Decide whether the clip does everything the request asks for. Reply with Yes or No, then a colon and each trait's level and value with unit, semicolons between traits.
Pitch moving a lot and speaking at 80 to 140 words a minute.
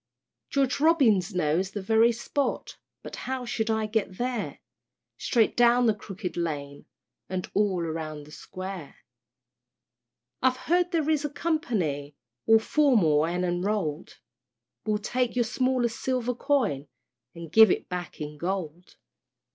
Yes: wide, 6.3 semitones; slow, 135 wpm